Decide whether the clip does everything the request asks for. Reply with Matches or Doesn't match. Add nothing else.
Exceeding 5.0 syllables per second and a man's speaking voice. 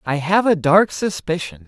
Doesn't match